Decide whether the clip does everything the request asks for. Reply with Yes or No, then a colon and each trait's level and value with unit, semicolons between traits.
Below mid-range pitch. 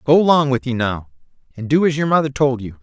Yes: low, 130 Hz